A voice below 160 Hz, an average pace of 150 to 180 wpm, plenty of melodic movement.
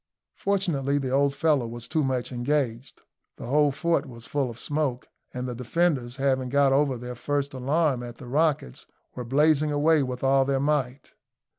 No: low, 135 Hz; average, 175 wpm; average, 2.8 semitones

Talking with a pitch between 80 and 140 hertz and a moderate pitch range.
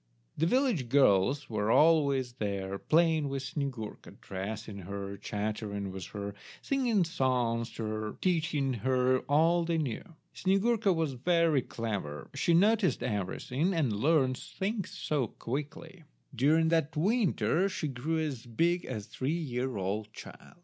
No: low, 135 Hz; wide, 7.2 semitones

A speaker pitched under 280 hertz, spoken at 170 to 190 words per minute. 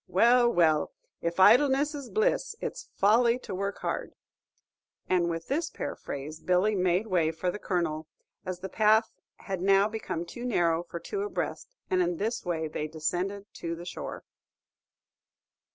No: medium, 185 Hz; average, 155 wpm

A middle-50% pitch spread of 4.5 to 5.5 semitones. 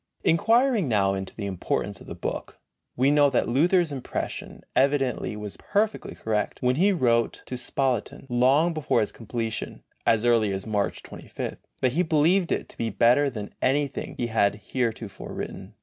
Yes: average, 5.1 semitones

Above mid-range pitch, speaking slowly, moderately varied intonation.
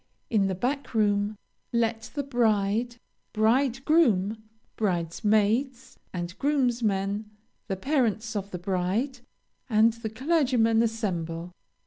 Yes: high, 220 Hz; slow, 100 wpm; average, 3.7 semitones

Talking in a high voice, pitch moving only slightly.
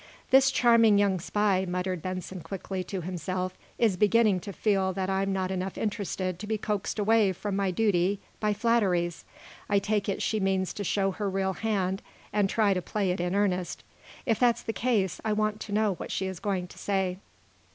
Yes: high, 195 Hz; narrow, 2.3 semitones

